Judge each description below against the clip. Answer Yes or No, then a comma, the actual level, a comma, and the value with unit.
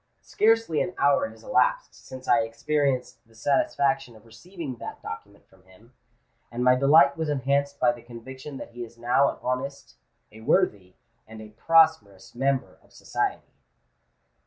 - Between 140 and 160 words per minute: Yes, average, 150 wpm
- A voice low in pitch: Yes, low, 130 Hz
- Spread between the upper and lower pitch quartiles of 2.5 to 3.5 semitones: No, average, 4.3 semitones